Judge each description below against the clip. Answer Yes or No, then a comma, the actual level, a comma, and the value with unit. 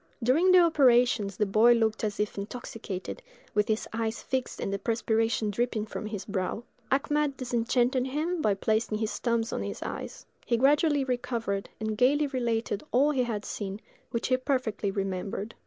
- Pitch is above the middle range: Yes, high, 230 Hz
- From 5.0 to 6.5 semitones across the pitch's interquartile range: No, average, 3.5 semitones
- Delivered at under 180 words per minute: Yes, average, 170 wpm